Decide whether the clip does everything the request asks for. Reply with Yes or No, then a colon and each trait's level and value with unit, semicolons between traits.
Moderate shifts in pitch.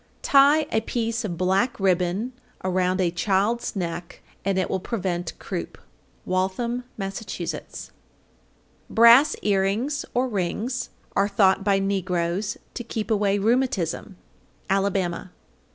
Yes: average, 3.9 semitones